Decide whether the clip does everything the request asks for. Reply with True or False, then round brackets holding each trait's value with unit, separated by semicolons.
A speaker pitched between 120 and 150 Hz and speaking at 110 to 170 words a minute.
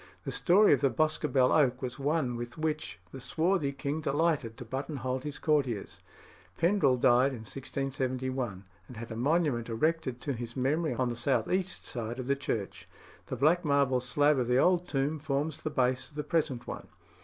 False (135 Hz; 185 wpm)